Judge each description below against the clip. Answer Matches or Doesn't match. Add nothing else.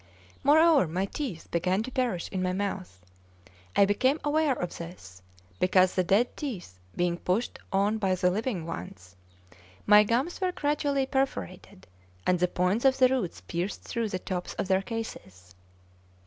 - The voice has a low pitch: Doesn't match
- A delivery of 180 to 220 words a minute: Doesn't match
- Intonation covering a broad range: Matches